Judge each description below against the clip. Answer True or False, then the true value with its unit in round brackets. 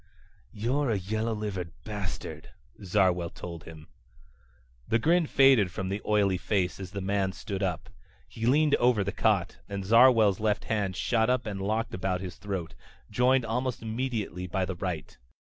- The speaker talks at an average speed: True (165 wpm)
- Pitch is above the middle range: False (100 Hz)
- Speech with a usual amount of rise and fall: True (3.5 semitones)